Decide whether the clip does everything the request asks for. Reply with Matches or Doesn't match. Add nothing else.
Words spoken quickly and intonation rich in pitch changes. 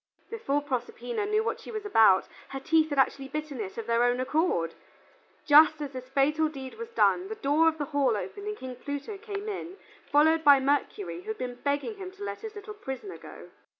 Matches